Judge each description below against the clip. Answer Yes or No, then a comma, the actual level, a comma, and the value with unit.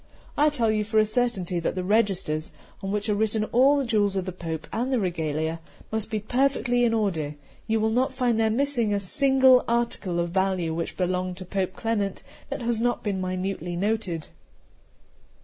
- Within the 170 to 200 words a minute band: Yes, average, 190 wpm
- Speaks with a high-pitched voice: Yes, high, 210 Hz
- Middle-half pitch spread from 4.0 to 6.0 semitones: Yes, average, 4.4 semitones